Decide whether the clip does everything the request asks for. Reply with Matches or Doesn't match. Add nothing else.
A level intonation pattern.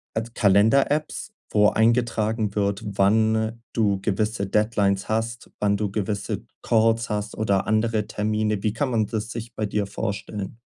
Matches